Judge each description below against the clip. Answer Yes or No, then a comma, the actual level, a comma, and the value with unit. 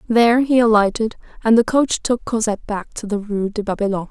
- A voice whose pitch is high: Yes, high, 220 Hz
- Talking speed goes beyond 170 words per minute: Yes, fast, 205 wpm